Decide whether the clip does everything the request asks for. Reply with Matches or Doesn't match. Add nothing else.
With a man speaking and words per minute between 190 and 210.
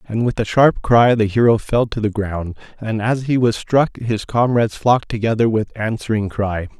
Matches